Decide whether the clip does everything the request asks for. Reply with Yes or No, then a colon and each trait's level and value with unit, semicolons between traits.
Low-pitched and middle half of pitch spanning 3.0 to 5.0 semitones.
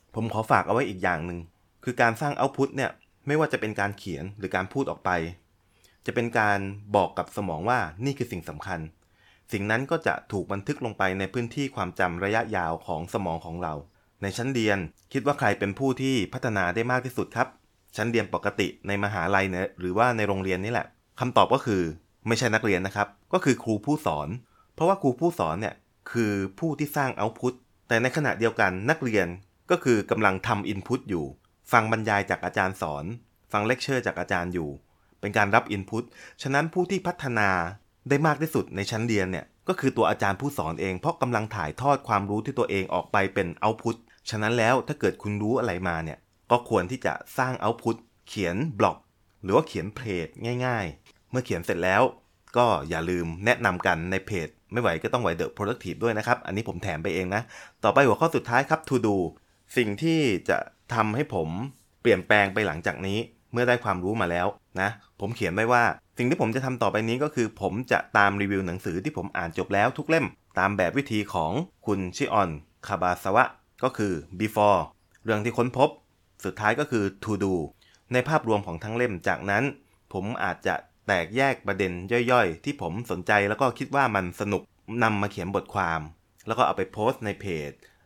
Yes: low, 105 Hz; average, 4.7 semitones